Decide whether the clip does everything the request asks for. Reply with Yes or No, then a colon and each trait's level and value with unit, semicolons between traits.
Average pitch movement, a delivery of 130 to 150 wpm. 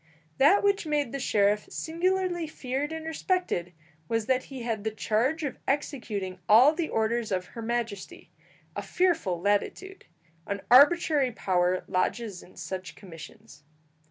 No: wide, 7.7 semitones; average, 140 wpm